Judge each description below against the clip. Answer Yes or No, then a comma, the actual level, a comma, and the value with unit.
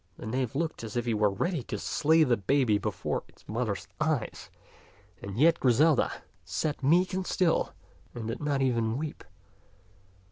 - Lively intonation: Yes, wide, 5.7 semitones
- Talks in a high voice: No, low, 130 Hz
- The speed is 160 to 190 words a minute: Yes, average, 165 wpm